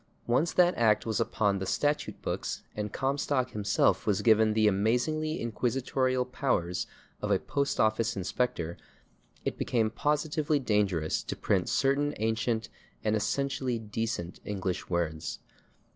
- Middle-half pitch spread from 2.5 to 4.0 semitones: No, average, 4.5 semitones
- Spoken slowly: Yes, slow, 130 wpm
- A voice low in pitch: Yes, low, 115 Hz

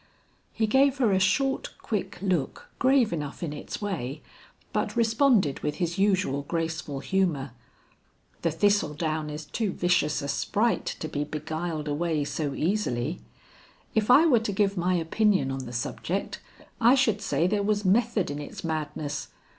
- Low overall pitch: No, medium, 175 Hz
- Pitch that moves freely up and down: Yes, wide, 5.9 semitones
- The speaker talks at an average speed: Yes, average, 160 wpm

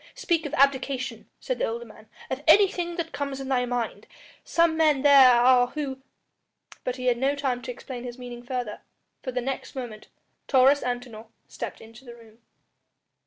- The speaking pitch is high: Yes, very high, 255 Hz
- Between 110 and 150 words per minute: No, average, 180 wpm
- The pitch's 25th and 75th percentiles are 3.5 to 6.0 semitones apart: No, narrow, 2.5 semitones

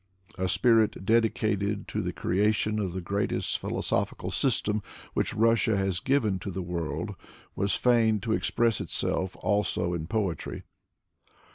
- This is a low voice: Yes, low, 105 Hz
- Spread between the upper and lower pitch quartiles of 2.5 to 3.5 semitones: Yes, average, 2.9 semitones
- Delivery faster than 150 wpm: No, average, 140 wpm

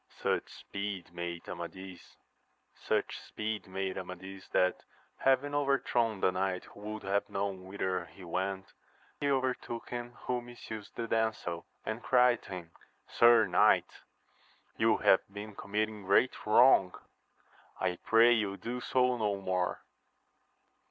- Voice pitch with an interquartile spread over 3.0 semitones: Yes, average, 4.1 semitones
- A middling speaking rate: No, slow, 125 wpm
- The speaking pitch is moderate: No, low, 100 Hz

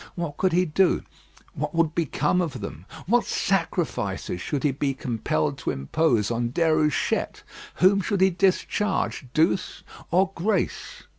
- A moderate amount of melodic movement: No, wide, 5.9 semitones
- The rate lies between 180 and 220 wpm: No, average, 140 wpm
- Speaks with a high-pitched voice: No, medium, 165 Hz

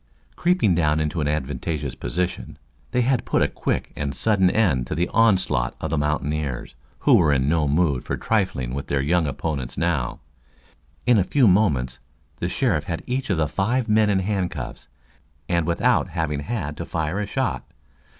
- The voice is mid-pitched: No, very low, 85 Hz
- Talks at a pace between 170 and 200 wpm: Yes, average, 180 wpm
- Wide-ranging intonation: Yes, wide, 6.0 semitones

